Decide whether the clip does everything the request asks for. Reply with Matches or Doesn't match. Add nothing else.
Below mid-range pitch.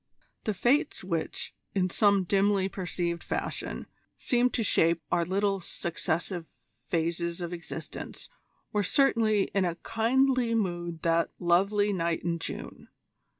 Doesn't match